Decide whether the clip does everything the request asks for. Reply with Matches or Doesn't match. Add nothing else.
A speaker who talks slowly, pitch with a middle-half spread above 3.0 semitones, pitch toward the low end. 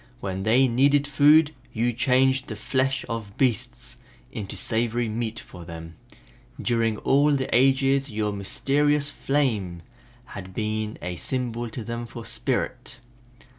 Matches